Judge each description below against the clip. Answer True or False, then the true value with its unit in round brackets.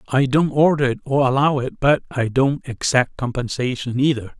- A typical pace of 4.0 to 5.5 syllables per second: True (5.0 syllables/s)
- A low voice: True (130 Hz)